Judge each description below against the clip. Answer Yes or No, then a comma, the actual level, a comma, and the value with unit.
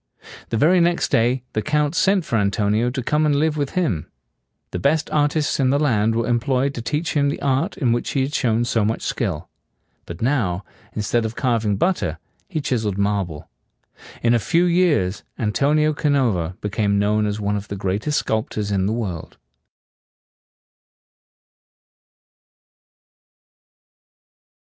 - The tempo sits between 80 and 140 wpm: No, average, 155 wpm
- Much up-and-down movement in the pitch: Yes, wide, 6.1 semitones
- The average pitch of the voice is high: No, low, 120 Hz